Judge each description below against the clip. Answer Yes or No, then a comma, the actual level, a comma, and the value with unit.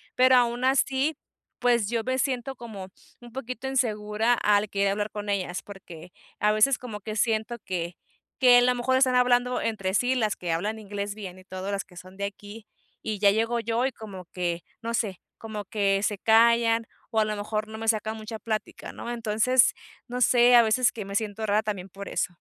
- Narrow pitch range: No, average, 3.1 semitones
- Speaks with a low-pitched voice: No, high, 220 Hz